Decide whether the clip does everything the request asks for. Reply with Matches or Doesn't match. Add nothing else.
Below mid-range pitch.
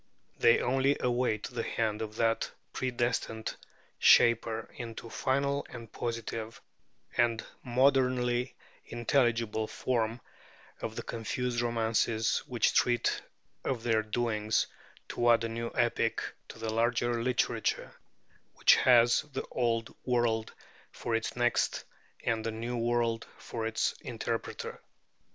Matches